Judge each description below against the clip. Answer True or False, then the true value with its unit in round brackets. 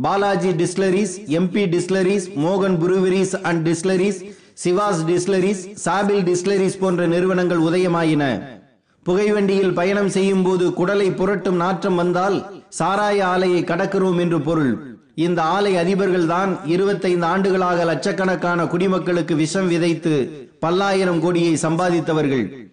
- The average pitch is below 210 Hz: True (185 Hz)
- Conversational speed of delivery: True (110 wpm)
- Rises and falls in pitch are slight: True (2.0 semitones)